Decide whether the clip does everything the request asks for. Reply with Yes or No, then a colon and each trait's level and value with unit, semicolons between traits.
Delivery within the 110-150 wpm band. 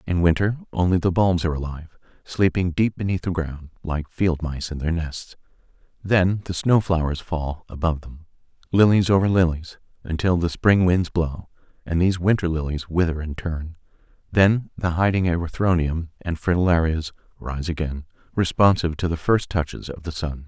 No: average, 165 wpm